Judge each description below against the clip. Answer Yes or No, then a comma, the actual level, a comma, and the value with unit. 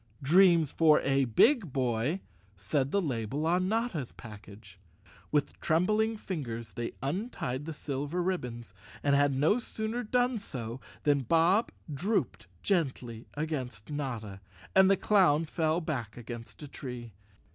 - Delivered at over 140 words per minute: No, slow, 135 wpm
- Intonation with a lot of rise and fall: Yes, wide, 7.1 semitones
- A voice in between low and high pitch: Yes, medium, 145 Hz